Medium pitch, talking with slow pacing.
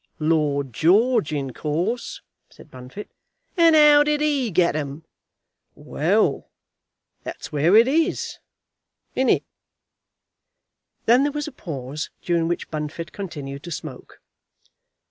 Yes: medium, 170 Hz; slow, 120 wpm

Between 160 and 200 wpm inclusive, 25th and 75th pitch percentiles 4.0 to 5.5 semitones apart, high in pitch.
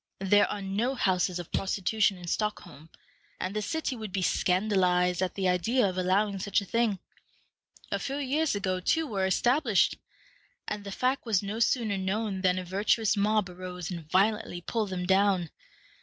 No: average, 170 wpm; average, 2.9 semitones; high, 195 Hz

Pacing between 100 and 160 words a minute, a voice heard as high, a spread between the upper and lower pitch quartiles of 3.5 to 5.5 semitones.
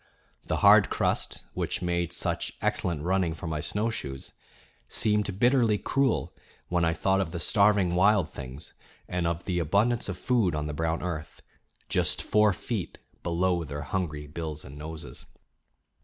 No: average, 155 wpm; very low, 90 Hz; average, 4.1 semitones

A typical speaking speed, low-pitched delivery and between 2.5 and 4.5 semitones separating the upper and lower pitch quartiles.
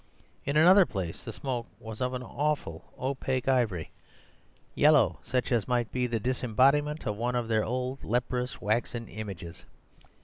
Yes: average, 150 wpm; low, 125 Hz; average, 2.8 semitones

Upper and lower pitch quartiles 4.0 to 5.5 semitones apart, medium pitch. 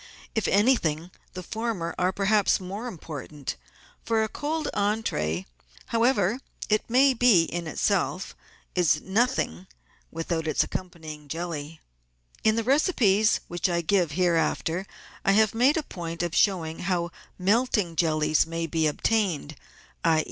Yes: average, 5.2 semitones; medium, 180 Hz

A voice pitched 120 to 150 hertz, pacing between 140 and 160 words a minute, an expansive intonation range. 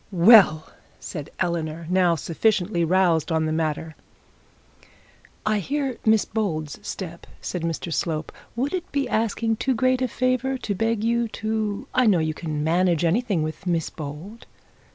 No: medium, 185 Hz; average, 155 wpm; wide, 5.8 semitones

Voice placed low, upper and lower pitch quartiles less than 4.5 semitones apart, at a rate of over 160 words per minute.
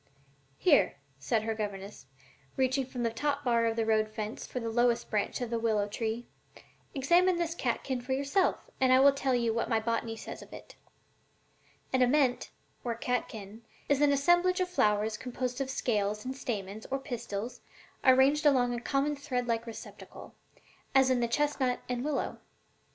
No: high, 245 Hz; average, 3.5 semitones; average, 175 wpm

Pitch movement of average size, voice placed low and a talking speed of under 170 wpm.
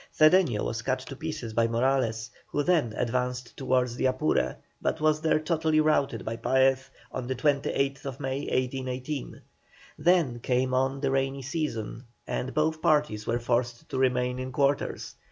Yes: average, 3.0 semitones; low, 130 Hz; average, 155 wpm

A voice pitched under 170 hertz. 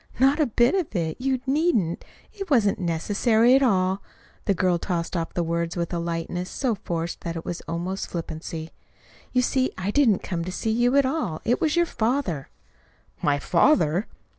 No: high, 190 Hz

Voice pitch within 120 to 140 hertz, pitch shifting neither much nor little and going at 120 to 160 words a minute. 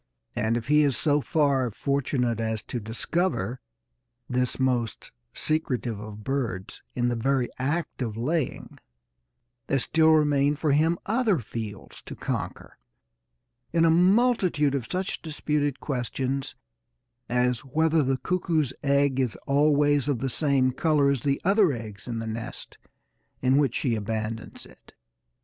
Yes: low, 135 Hz; average, 4.1 semitones; average, 140 wpm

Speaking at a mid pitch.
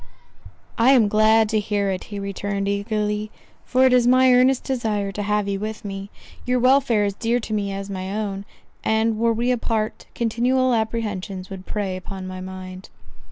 No: high, 210 Hz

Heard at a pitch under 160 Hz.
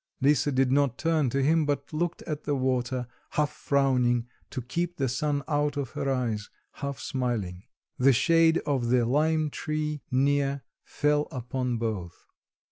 Yes: medium, 140 Hz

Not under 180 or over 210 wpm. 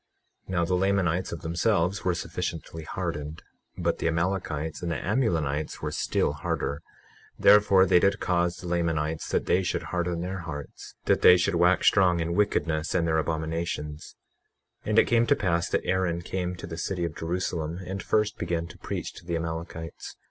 Yes: average, 185 wpm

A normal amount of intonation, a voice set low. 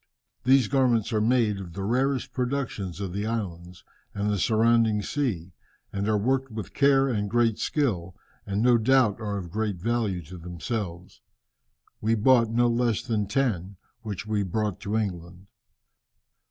Yes: average, 3.6 semitones; low, 110 Hz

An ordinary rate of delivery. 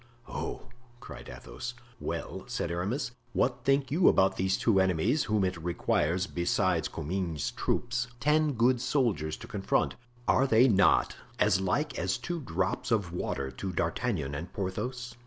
Yes: average, 150 wpm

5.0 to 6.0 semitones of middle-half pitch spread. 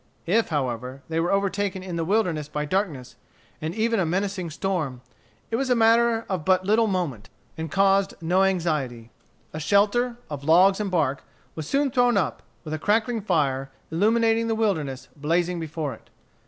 Yes: wide, 5.6 semitones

